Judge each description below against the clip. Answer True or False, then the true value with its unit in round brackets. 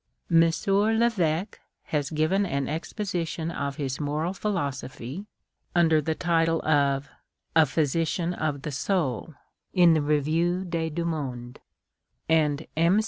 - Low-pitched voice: False (160 Hz)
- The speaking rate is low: True (130 wpm)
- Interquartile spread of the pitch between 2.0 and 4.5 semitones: True (3.1 semitones)